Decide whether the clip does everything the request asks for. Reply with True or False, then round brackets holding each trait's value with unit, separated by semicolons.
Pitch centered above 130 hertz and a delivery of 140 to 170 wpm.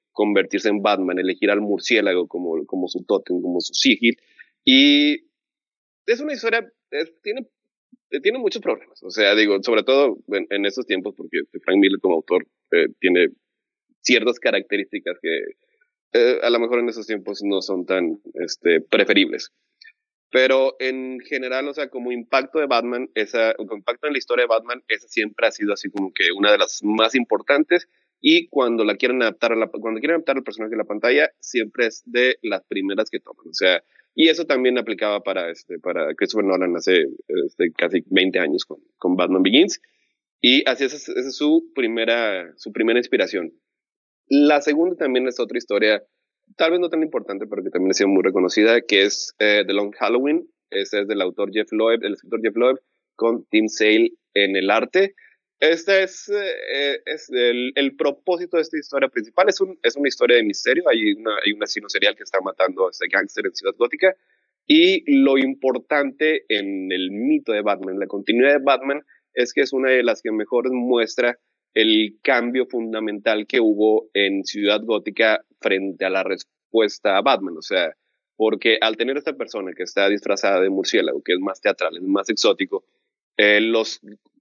False (140 Hz; 185 wpm)